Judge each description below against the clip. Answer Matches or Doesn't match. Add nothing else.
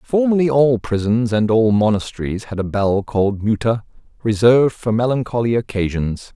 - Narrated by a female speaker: Doesn't match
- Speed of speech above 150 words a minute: Doesn't match